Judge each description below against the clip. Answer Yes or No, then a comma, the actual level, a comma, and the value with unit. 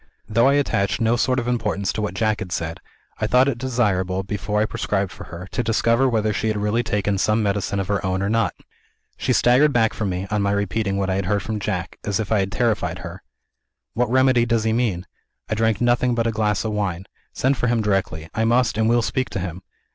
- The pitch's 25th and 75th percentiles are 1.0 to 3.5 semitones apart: Yes, average, 3.0 semitones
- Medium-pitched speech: No, low, 110 Hz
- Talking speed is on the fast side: Yes, fast, 240 wpm